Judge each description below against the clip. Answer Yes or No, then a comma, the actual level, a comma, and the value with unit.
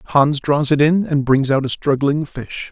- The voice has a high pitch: No, medium, 140 Hz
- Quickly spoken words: Yes, fast, 220 wpm